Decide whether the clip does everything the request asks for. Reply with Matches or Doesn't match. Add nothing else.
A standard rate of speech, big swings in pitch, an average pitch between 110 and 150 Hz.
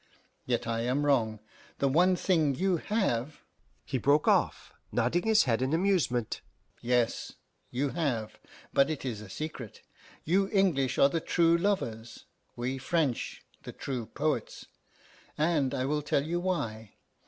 Matches